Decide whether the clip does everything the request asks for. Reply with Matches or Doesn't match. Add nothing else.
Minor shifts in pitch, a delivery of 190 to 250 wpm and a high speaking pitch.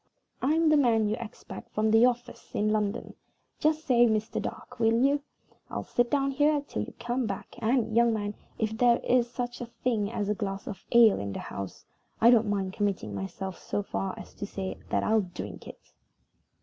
Doesn't match